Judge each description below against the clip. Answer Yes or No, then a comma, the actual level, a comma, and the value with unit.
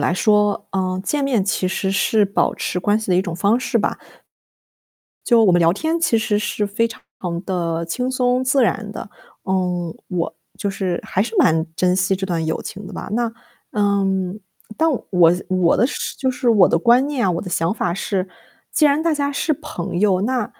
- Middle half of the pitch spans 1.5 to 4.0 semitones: No, average, 4.6 semitones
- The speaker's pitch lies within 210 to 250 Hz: No, high, 200 Hz